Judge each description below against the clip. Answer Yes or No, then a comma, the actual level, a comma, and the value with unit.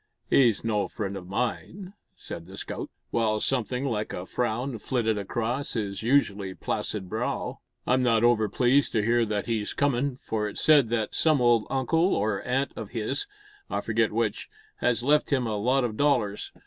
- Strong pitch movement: No, average, 3.7 semitones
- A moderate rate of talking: Yes, average, 175 wpm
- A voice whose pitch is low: Yes, low, 115 Hz